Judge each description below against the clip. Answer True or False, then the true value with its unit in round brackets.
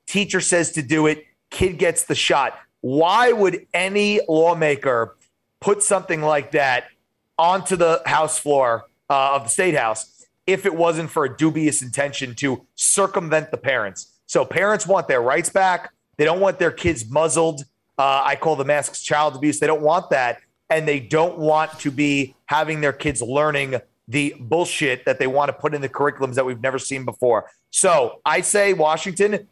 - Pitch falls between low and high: True (155 Hz)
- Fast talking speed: False (180 wpm)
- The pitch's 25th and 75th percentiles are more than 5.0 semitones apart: False (3.7 semitones)